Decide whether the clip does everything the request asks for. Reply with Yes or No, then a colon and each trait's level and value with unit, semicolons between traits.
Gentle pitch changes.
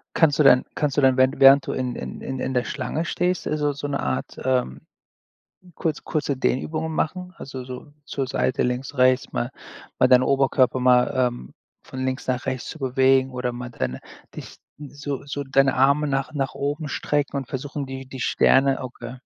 Yes: narrow, 2.0 semitones